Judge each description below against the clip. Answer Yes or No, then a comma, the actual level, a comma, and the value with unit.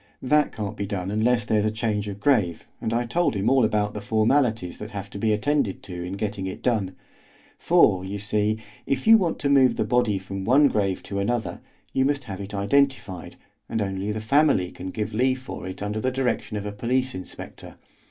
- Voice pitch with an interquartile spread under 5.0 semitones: Yes, average, 4.2 semitones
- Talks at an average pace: No, fast, 215 wpm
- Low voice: Yes, low, 110 Hz